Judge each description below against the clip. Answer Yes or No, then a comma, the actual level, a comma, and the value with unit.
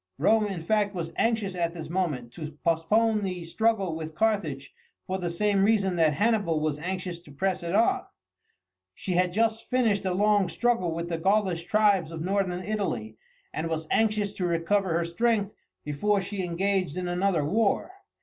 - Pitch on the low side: No, medium, 185 Hz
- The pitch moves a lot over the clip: No, average, 3.8 semitones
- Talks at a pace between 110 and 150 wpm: No, average, 180 wpm